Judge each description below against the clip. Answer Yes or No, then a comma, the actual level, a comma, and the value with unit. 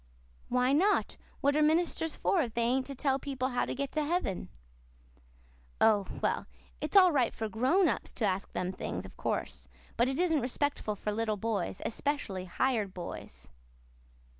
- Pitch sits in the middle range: No, very high, 255 Hz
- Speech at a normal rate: Yes, average, 170 wpm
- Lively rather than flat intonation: Yes, wide, 5.8 semitones